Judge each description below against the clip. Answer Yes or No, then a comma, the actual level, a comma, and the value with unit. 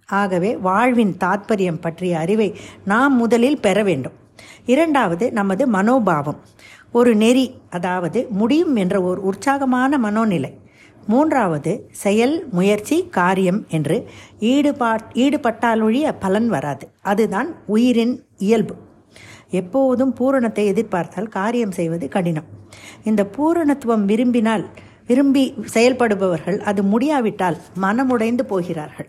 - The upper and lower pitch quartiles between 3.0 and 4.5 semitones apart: No, average, 5.2 semitones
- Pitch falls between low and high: No, high, 210 Hz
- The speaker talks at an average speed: Yes, average, 95 wpm